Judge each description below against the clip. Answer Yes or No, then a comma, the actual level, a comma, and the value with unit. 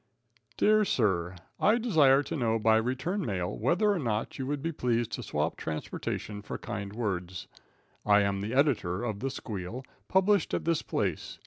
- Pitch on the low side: Yes, low, 120 Hz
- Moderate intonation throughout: No, wide, 6.6 semitones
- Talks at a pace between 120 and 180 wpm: Yes, average, 175 wpm